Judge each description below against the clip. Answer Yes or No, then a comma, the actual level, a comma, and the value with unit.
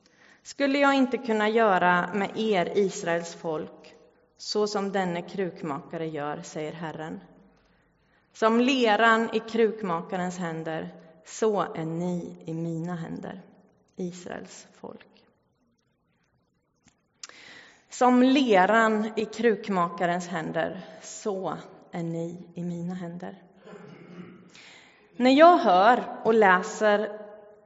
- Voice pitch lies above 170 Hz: Yes, high, 190 Hz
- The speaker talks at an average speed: No, slow, 100 wpm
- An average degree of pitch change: Yes, average, 4.2 semitones